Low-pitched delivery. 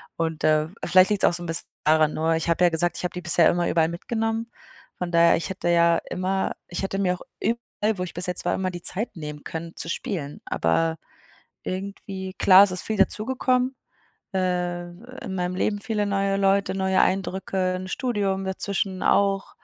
No: medium, 185 Hz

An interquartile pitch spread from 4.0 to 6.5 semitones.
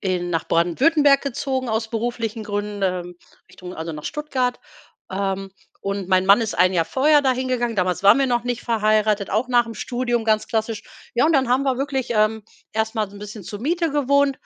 Yes: average, 4.5 semitones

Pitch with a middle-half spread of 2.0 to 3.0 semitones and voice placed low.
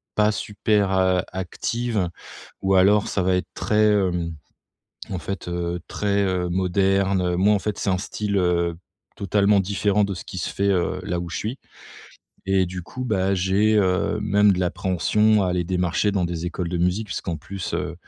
Yes: narrow, 2.4 semitones; very low, 95 Hz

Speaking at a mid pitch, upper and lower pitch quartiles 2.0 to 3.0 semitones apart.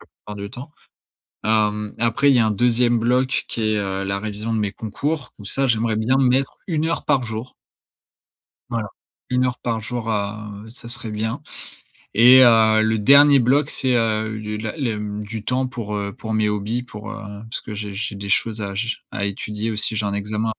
No: low, 110 Hz; average, 2.7 semitones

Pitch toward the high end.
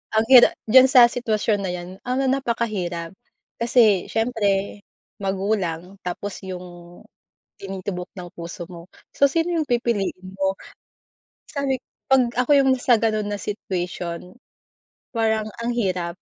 Yes: high, 205 Hz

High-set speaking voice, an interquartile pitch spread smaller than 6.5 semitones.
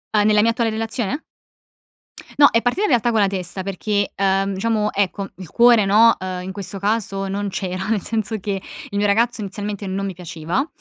Yes: high, 205 Hz; average, 2.7 semitones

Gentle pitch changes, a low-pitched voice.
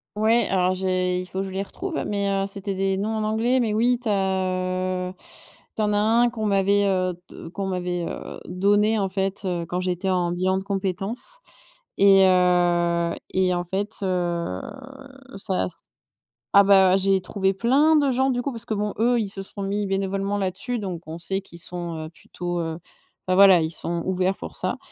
No: narrow, 2.2 semitones; high, 195 Hz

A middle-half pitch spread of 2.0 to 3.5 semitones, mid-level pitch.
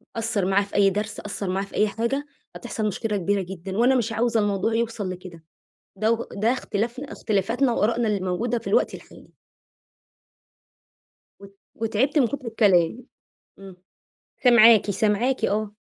No: average, 2.9 semitones; high, 215 Hz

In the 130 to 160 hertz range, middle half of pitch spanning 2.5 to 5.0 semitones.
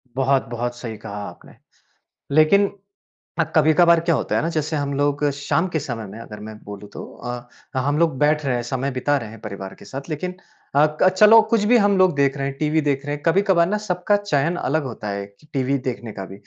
No: medium, 140 Hz; wide, 5.4 semitones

